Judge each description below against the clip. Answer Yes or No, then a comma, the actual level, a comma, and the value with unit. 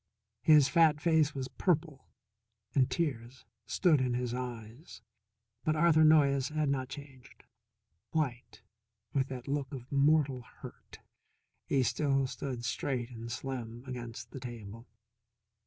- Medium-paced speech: No, slow, 125 wpm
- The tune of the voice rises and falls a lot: No, average, 3.4 semitones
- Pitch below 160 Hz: Yes, low, 135 Hz